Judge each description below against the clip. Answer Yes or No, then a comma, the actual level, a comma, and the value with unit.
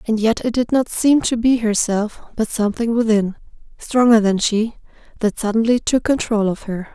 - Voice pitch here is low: No, high, 225 Hz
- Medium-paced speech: Yes, average, 180 wpm